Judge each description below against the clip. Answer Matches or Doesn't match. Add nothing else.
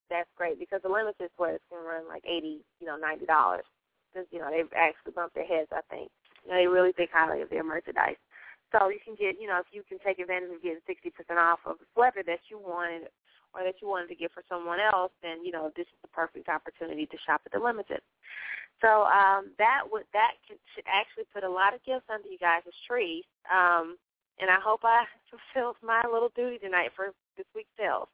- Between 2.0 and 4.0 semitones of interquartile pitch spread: Doesn't match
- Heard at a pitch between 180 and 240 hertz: Matches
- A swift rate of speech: Matches